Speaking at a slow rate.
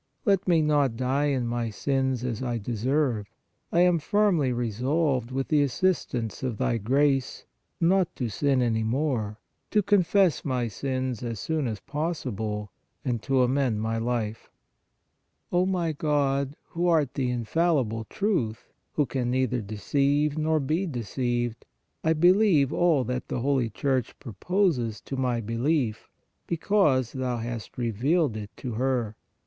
No: average, 145 wpm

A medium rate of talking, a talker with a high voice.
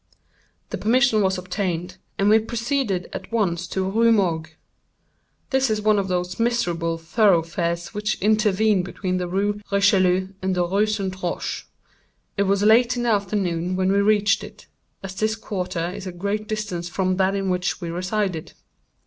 Yes: average, 175 wpm; high, 195 Hz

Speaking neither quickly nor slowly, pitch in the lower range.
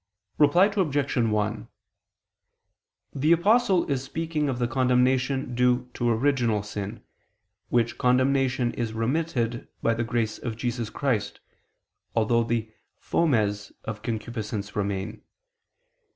No: slow, 110 wpm; low, 120 Hz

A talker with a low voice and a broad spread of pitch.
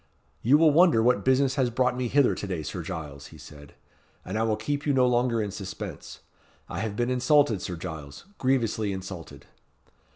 Yes: low, 115 Hz; wide, 5.7 semitones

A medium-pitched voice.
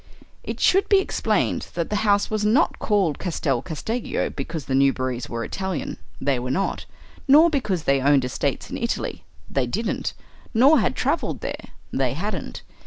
Yes: medium, 175 Hz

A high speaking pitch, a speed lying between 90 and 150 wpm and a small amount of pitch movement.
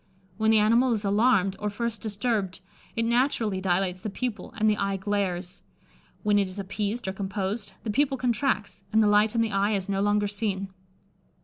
No: high, 205 Hz; average, 190 wpm; narrow, 2.3 semitones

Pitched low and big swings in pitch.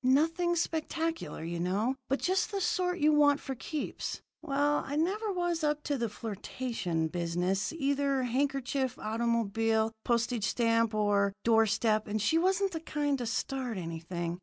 No: very high, 255 Hz; wide, 6.1 semitones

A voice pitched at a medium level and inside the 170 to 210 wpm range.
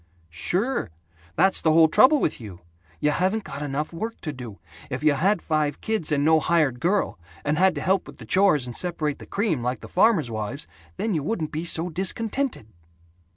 Yes: medium, 160 Hz; average, 200 wpm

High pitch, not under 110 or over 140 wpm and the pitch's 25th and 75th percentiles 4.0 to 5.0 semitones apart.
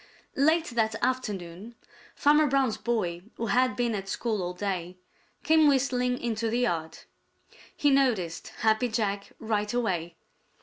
Yes: high, 225 Hz; slow, 135 wpm; average, 4.4 semitones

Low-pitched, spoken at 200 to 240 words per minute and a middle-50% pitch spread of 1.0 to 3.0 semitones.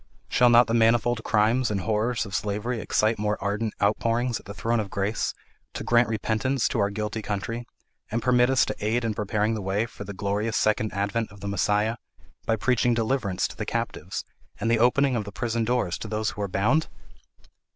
Yes: low, 110 Hz; fast, 205 wpm; narrow, 2.4 semitones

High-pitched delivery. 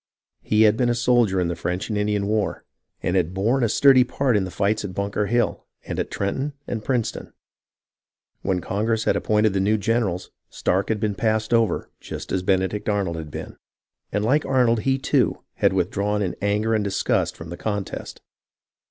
No: low, 105 Hz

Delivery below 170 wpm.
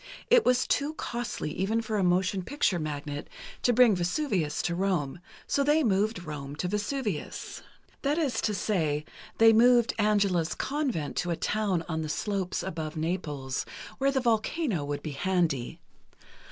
Yes: average, 155 wpm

